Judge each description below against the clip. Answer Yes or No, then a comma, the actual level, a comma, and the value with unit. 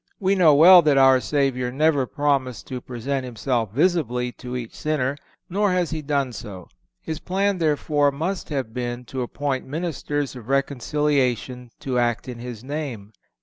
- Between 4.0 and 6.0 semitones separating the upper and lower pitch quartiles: No, average, 3.5 semitones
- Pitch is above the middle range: No, low, 135 Hz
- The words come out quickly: No, average, 160 wpm